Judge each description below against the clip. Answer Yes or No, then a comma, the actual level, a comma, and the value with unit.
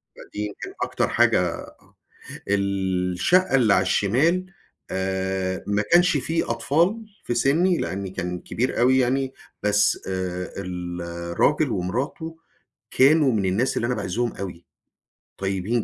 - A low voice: Yes, low, 105 Hz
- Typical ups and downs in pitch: No, wide, 6.2 semitones